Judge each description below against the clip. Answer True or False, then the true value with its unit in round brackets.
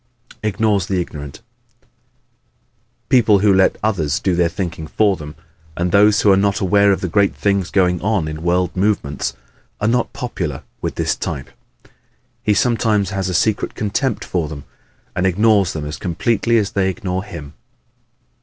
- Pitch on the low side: True (95 Hz)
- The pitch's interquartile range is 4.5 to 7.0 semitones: False (3.3 semitones)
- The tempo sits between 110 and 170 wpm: True (165 wpm)